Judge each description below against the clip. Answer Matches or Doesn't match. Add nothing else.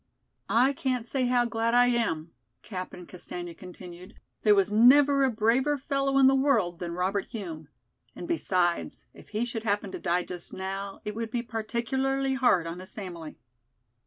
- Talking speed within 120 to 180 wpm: Matches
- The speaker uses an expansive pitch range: Matches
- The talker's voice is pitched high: Matches